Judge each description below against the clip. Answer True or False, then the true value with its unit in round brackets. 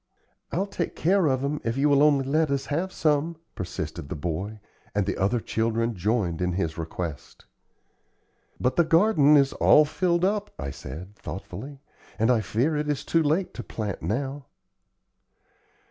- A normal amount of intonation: False (7.5 semitones)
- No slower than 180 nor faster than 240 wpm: False (165 wpm)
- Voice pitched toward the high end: False (135 Hz)